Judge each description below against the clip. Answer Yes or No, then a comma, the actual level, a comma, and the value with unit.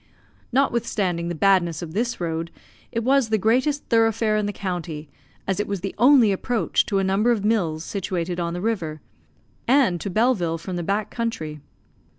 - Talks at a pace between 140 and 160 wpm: No, average, 175 wpm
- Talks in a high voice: Yes, high, 200 Hz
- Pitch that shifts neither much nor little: Yes, average, 4.8 semitones